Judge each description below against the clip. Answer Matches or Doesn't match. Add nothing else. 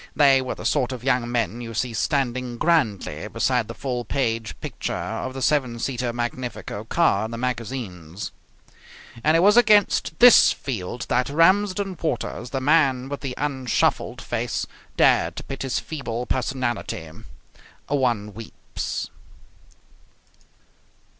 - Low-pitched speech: Matches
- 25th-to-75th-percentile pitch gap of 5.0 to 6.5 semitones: Doesn't match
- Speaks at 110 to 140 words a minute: Matches